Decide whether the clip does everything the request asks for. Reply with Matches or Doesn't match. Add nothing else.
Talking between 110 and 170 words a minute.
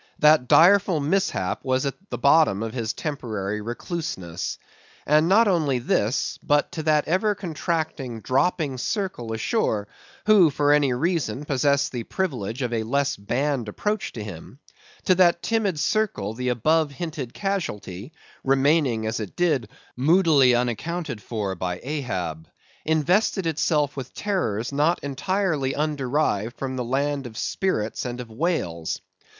Matches